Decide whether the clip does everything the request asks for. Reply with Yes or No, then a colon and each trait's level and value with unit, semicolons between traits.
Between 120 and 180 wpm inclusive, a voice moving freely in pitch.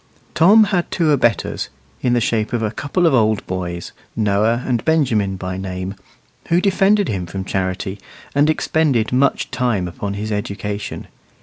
Yes: average, 160 wpm; wide, 7.0 semitones